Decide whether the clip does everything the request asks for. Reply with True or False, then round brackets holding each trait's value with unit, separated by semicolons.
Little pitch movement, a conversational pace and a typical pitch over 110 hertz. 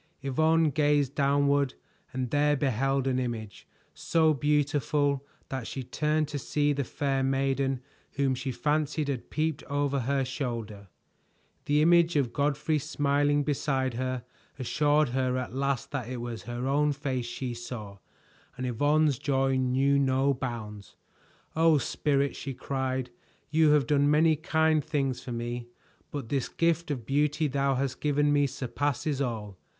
True (2.3 semitones; 150 wpm; 140 Hz)